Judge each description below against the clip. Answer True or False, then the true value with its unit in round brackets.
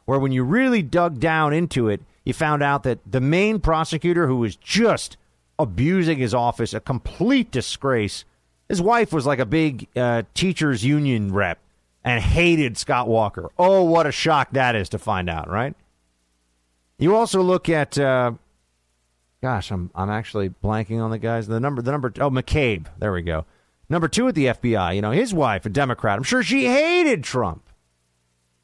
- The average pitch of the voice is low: True (125 Hz)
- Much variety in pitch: True (8.3 semitones)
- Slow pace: False (180 wpm)